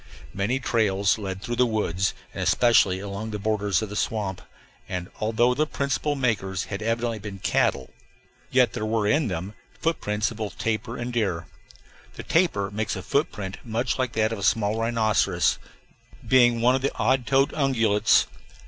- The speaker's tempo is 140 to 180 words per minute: Yes, average, 170 wpm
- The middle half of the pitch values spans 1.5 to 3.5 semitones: Yes, average, 3.2 semitones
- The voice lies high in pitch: No, low, 110 Hz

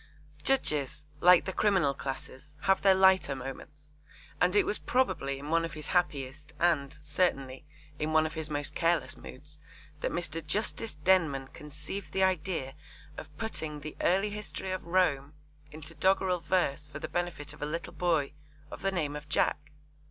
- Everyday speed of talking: Yes, average, 165 wpm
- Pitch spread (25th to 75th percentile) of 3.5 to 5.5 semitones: Yes, average, 4.0 semitones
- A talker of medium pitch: Yes, medium, 155 Hz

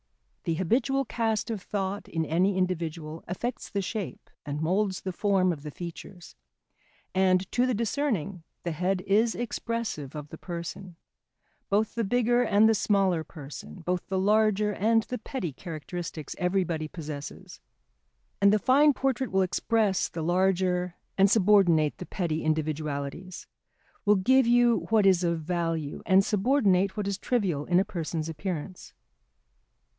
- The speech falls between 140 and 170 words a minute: Yes, average, 150 wpm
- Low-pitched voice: No, high, 190 Hz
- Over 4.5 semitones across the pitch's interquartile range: No, average, 4.2 semitones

